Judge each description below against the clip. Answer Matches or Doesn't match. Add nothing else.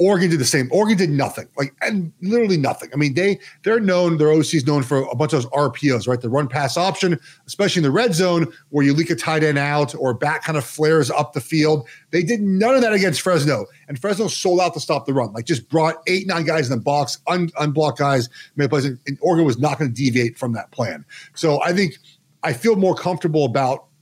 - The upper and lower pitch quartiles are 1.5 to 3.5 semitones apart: Doesn't match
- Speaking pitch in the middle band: Matches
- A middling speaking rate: Doesn't match